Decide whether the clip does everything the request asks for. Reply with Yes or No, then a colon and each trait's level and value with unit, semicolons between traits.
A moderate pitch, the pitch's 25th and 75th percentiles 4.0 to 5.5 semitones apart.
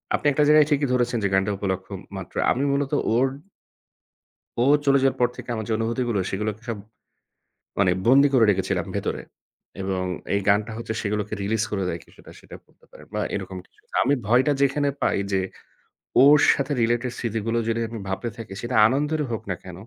No: low, 115 Hz; average, 4.7 semitones